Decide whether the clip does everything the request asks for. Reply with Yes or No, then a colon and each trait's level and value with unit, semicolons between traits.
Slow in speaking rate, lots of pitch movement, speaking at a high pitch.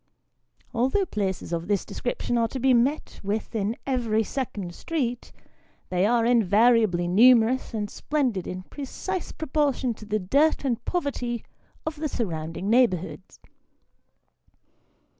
No: slow, 130 wpm; average, 4.6 semitones; high, 235 Hz